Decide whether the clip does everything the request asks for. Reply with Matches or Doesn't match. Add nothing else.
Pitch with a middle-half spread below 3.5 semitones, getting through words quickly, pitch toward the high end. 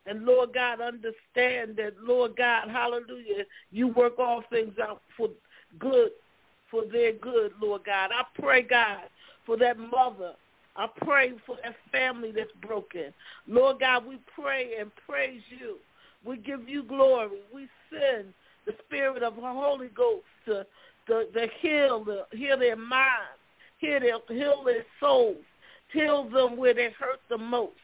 Doesn't match